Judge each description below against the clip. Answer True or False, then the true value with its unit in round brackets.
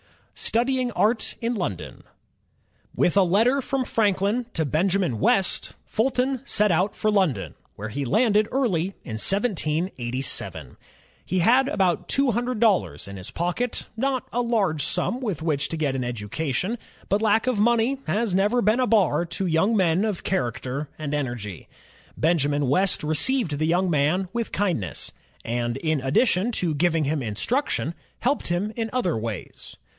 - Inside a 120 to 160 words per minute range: True (155 wpm)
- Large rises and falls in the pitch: True (7.5 semitones)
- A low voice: False (185 Hz)